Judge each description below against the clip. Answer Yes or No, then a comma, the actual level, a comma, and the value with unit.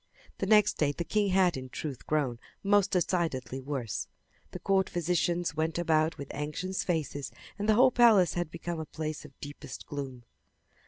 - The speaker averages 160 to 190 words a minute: Yes, average, 170 wpm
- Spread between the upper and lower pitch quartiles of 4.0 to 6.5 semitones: Yes, average, 4.6 semitones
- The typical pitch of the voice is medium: Yes, medium, 165 Hz